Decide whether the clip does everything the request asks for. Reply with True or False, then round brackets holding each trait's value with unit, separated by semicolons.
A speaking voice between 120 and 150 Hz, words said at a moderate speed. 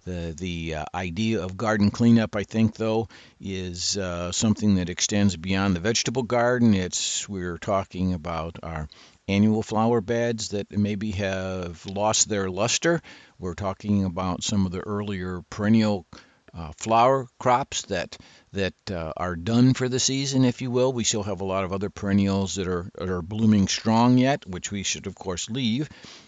False (100 Hz; 175 wpm)